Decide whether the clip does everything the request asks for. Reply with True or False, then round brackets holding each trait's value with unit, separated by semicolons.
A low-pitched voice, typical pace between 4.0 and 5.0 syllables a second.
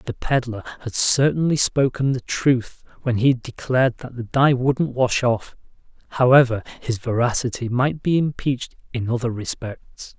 True (125 Hz; 4.6 syllables/s)